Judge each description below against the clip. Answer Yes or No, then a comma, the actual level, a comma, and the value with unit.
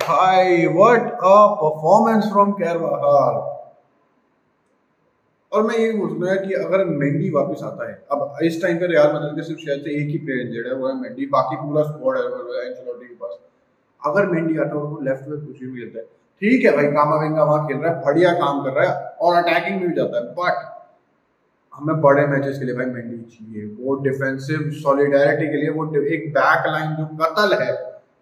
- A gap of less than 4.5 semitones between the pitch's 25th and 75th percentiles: No, average, 5.3 semitones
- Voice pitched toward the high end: No, medium, 155 Hz